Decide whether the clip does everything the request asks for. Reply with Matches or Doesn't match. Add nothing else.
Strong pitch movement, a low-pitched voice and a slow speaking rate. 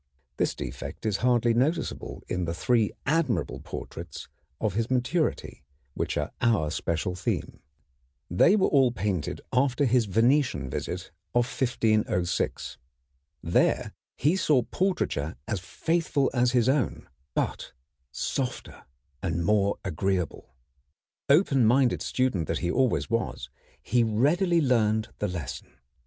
Matches